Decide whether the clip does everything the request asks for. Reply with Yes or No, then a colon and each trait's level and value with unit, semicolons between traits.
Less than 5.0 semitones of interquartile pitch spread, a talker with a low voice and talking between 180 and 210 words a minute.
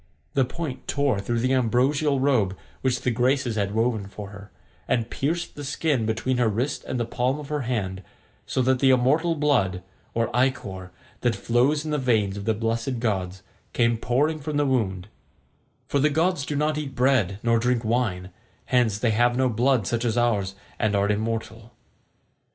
Yes: average, 3.7 semitones; low, 120 Hz; average, 185 wpm